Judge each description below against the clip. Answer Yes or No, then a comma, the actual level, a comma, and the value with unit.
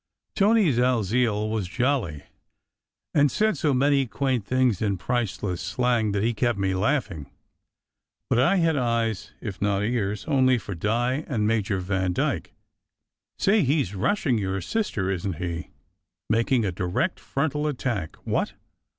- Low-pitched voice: Yes, low, 115 Hz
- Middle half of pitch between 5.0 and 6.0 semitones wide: Yes, wide, 5.4 semitones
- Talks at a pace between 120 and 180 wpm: Yes, average, 145 wpm